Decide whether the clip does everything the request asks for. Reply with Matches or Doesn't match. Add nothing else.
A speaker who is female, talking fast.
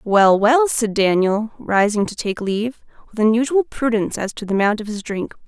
Doesn't match